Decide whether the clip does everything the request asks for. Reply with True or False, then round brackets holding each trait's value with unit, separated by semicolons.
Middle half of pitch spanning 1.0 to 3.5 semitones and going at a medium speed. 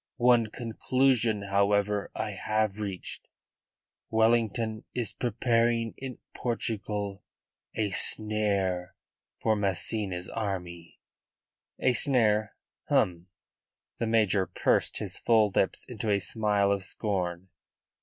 False (2.6 semitones; 100 wpm)